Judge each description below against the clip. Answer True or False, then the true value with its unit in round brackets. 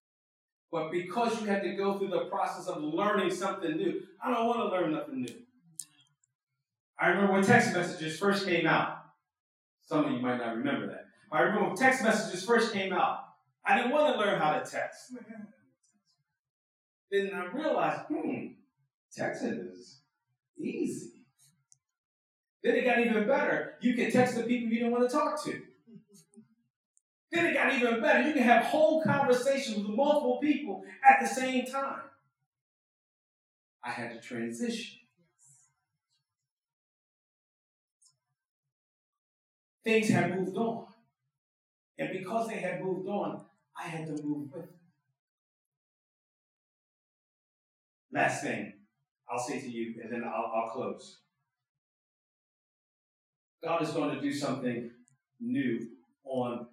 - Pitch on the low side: False (185 Hz)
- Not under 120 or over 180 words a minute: True (140 wpm)